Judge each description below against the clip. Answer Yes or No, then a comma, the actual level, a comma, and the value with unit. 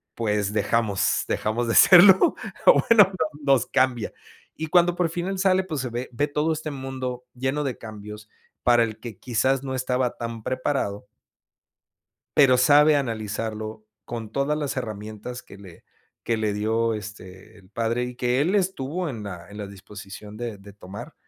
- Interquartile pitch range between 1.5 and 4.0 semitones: No, average, 4.6 semitones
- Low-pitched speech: Yes, low, 120 Hz